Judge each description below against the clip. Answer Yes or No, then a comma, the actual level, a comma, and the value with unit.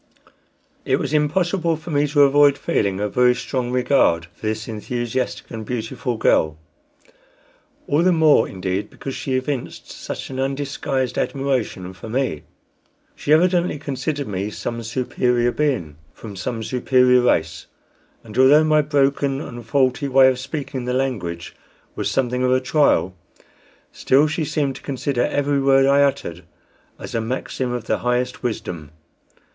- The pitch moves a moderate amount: Yes, average, 3.7 semitones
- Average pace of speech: Yes, average, 150 wpm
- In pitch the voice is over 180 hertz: No, low, 130 Hz